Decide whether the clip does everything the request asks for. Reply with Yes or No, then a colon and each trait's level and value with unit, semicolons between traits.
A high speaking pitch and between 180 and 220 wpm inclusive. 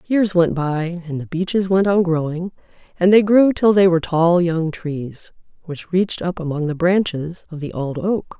No: medium, 175 Hz; average, 200 wpm